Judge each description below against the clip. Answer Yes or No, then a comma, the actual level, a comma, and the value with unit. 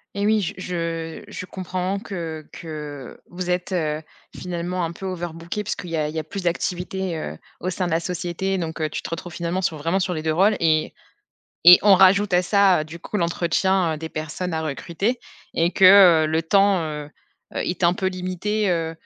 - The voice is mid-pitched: Yes, medium, 175 Hz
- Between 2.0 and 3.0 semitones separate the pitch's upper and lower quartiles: Yes, narrow, 2.6 semitones